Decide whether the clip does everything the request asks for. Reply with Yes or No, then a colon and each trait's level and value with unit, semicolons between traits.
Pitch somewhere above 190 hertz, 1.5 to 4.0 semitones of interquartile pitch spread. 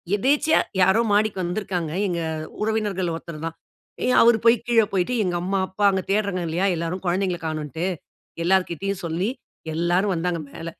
No: medium, 185 Hz; average, 3.2 semitones